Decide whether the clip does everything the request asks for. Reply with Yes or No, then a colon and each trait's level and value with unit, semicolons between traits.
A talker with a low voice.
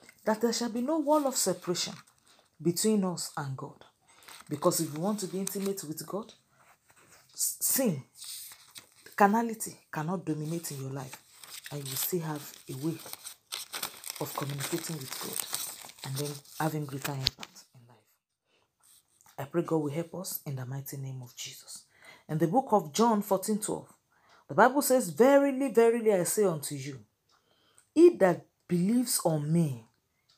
No: medium, 170 Hz